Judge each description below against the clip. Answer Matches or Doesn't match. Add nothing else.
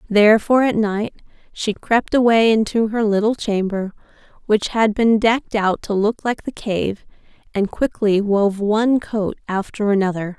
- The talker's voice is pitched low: Doesn't match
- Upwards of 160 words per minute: Doesn't match